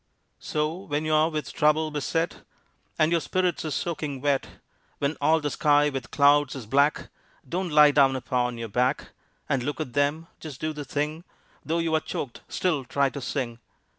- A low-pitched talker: No, medium, 145 Hz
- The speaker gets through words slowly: No, average, 180 wpm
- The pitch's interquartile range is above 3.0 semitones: No, narrow, 2.5 semitones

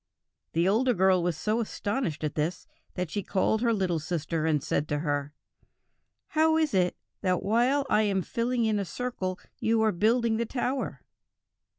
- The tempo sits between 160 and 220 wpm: Yes, average, 175 wpm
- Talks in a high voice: Yes, high, 205 Hz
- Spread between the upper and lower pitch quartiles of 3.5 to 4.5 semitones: No, average, 5.2 semitones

